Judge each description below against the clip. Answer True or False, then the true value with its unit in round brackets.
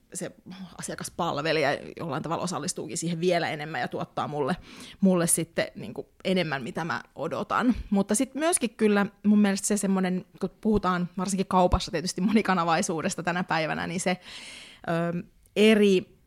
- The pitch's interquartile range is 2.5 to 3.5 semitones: True (2.8 semitones)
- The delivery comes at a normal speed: True (140 wpm)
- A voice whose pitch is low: False (185 Hz)